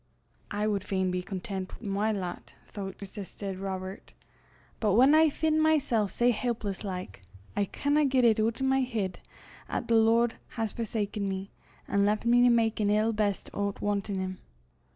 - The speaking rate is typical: Yes, average, 180 wpm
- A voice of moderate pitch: No, high, 210 Hz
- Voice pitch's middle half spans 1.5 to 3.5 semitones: Yes, average, 3.2 semitones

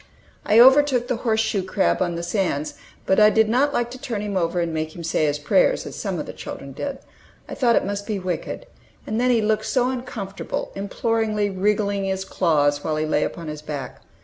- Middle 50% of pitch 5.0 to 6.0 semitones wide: Yes, average, 5.3 semitones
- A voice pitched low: No, high, 205 Hz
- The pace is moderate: No, fast, 220 wpm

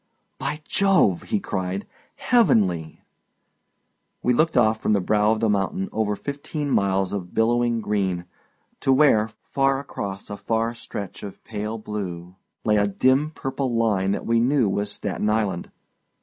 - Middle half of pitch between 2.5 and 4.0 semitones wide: No, average, 4.7 semitones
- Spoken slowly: No, average, 150 wpm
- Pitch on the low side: Yes, low, 110 Hz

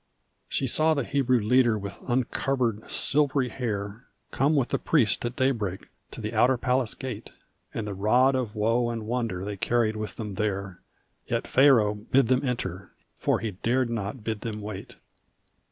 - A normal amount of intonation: Yes, average, 3.6 semitones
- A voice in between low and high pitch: No, low, 115 Hz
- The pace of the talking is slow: No, average, 170 wpm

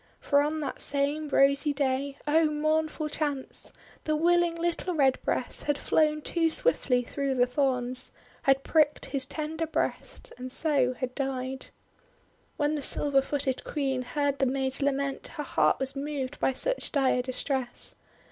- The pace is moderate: Yes, average, 155 wpm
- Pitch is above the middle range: Yes, very high, 280 Hz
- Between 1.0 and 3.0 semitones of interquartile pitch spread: Yes, narrow, 2.4 semitones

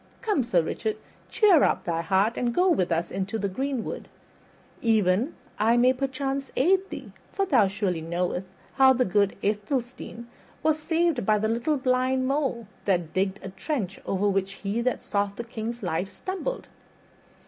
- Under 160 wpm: No, average, 165 wpm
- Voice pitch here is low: No, high, 230 Hz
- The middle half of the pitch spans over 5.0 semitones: Yes, wide, 5.6 semitones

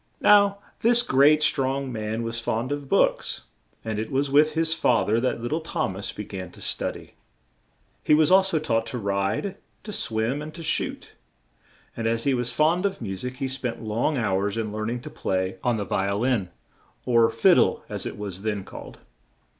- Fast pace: Yes, fast, 210 wpm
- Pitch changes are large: Yes, wide, 5.7 semitones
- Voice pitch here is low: Yes, low, 120 Hz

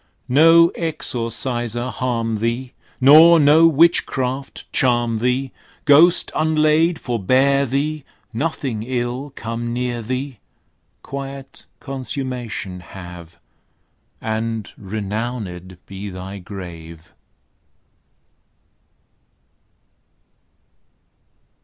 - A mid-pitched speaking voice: No, low, 125 Hz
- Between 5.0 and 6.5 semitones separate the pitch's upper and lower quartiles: No, average, 4.1 semitones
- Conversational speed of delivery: No, slow, 70 wpm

